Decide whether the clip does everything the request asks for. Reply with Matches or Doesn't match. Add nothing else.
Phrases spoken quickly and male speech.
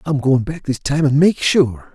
Matches